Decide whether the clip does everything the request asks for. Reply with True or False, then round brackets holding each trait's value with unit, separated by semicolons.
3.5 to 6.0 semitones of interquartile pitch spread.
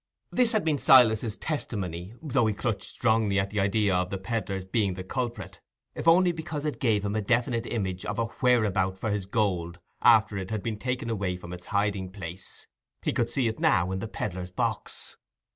True (4.0 semitones)